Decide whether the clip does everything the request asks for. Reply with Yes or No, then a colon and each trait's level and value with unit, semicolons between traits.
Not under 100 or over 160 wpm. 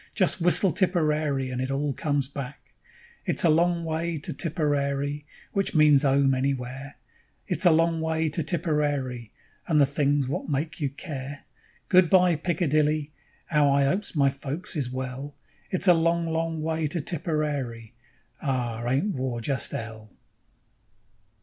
Yes: average, 150 wpm